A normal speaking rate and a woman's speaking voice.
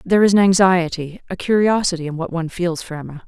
No: fast, 220 wpm; female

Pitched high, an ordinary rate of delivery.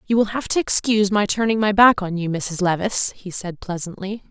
No: high, 200 Hz; fast, 225 wpm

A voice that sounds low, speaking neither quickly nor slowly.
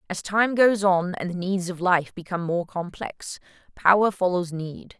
No: medium, 185 Hz; average, 180 wpm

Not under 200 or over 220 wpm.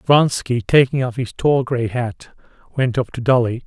No: average, 180 wpm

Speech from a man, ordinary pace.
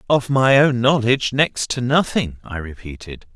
Yes: male; average, 160 wpm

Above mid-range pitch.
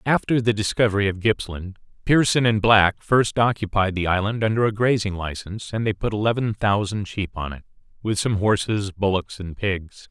No: low, 105 Hz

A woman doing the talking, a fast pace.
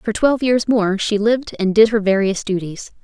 Yes: female; fast, 220 wpm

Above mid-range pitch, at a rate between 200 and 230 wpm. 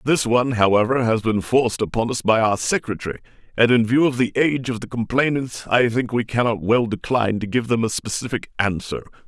No: low, 120 Hz; fast, 205 wpm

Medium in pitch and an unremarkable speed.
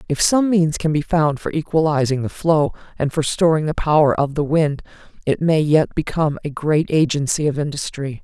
Yes: medium, 150 Hz; average, 195 wpm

